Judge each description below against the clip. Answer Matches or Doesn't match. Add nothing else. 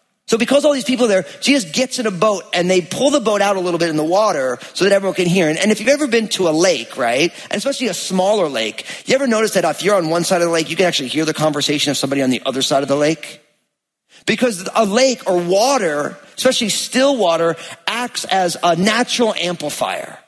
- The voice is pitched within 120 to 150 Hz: Doesn't match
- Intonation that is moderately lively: Doesn't match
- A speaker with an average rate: Doesn't match